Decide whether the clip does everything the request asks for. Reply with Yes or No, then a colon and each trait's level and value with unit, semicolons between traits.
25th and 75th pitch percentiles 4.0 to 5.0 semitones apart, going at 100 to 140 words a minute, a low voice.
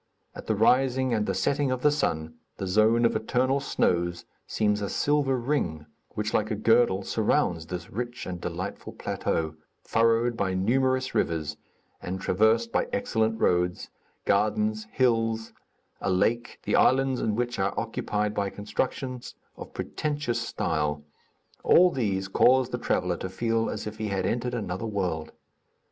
No: average, 4.5 semitones; average, 155 wpm; low, 110 Hz